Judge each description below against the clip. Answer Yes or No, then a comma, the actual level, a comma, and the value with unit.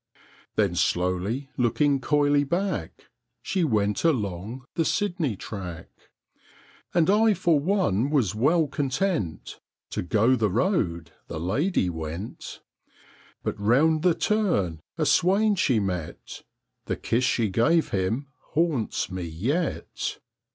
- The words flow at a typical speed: No, slow, 120 wpm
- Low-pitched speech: Yes, low, 130 Hz